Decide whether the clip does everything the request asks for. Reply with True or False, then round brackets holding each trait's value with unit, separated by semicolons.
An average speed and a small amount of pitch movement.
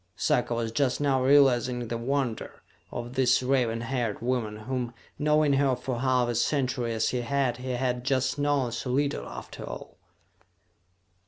True (160 wpm; 2.1 semitones)